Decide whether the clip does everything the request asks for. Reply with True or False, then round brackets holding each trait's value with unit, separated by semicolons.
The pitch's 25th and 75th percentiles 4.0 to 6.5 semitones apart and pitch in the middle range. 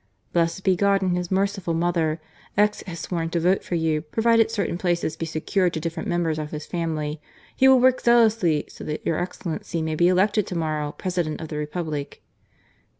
False (3.2 semitones; 170 Hz)